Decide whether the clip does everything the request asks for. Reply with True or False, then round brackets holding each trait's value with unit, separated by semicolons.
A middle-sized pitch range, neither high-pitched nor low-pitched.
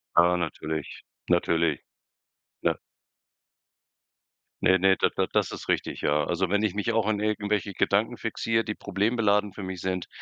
False (3.3 semitones; 100 Hz)